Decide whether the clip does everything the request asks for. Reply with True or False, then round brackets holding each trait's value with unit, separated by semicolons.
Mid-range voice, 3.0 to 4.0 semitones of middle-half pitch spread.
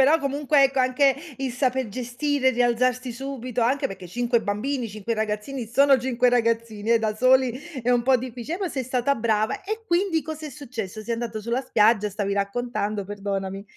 False (245 Hz; 3.6 semitones)